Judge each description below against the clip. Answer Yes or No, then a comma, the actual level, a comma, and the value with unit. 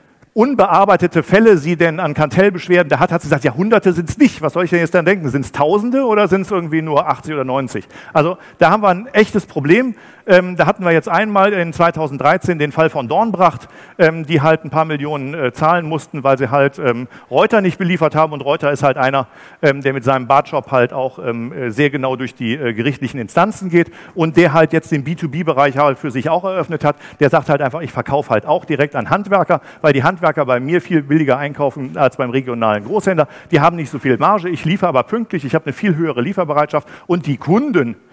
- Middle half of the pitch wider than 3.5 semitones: Yes, average, 4.2 semitones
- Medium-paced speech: No, fast, 230 wpm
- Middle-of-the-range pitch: Yes, medium, 160 Hz